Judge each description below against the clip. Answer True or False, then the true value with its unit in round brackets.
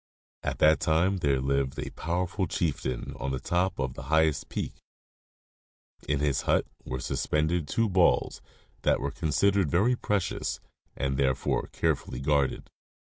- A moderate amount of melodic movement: True (4.5 semitones)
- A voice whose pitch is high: False (75 Hz)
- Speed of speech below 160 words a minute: True (145 wpm)